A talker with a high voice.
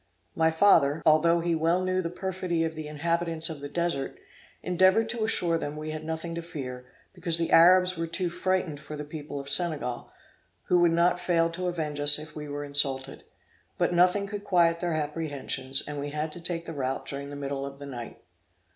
No: medium, 165 Hz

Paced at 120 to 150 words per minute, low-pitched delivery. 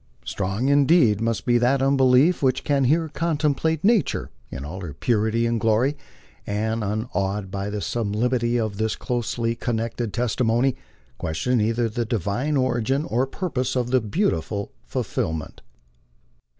Yes: average, 140 wpm; low, 120 Hz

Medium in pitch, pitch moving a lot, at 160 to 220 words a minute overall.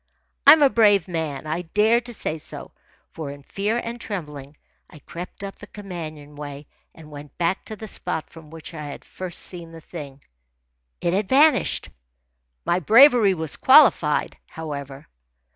Yes: medium, 170 Hz; wide, 5.7 semitones; average, 165 wpm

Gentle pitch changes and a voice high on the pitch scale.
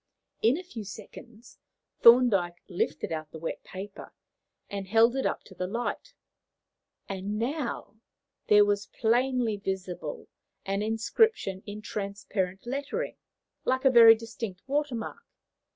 No: average, 4.1 semitones; high, 220 Hz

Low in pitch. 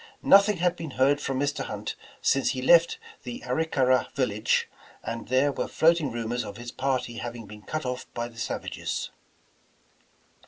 Yes: low, 130 Hz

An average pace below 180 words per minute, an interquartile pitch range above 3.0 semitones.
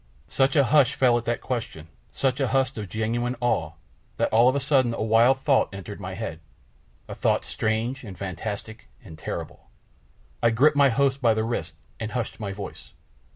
No: average, 190 wpm; average, 3.7 semitones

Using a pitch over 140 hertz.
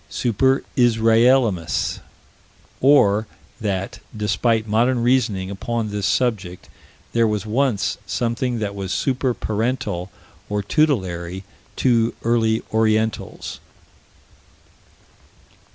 No: low, 110 Hz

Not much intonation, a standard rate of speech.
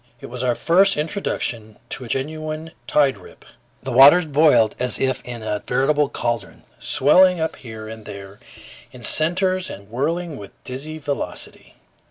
No: average, 5.1 semitones; average, 155 wpm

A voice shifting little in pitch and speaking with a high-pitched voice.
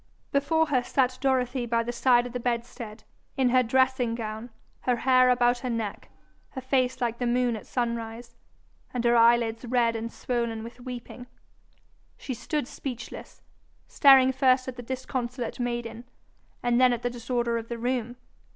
Yes: narrow, 1.5 semitones; high, 245 Hz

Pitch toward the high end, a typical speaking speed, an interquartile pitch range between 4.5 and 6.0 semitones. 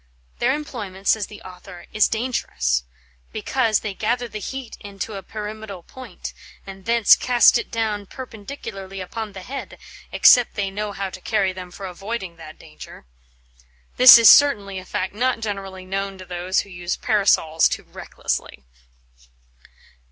No: high, 200 Hz; average, 150 wpm; average, 3.3 semitones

